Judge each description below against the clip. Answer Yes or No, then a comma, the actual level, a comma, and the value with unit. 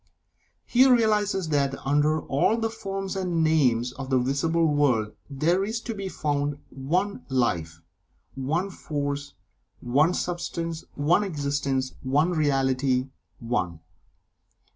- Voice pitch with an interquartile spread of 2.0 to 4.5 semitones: No, average, 5.0 semitones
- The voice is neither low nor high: Yes, medium, 145 Hz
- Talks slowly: Yes, slow, 120 wpm